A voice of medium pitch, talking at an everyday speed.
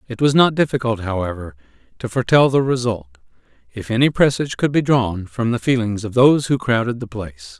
No: low, 115 Hz; average, 190 wpm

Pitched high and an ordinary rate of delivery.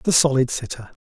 No: medium, 140 Hz; average, 175 wpm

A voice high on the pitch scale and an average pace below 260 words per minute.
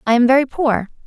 Yes: very high, 255 Hz; fast, 225 wpm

